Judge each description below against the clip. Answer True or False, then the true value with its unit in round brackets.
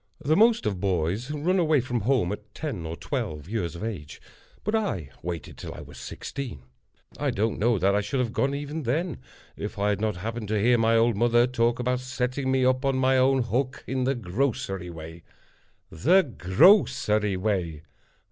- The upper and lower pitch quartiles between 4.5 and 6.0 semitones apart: True (5.2 semitones)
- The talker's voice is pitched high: False (115 Hz)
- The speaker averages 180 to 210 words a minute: True (190 wpm)